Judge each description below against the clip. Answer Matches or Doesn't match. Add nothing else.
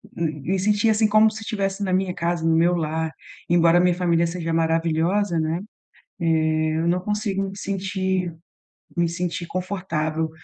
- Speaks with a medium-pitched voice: Matches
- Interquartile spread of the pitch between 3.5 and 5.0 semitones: Doesn't match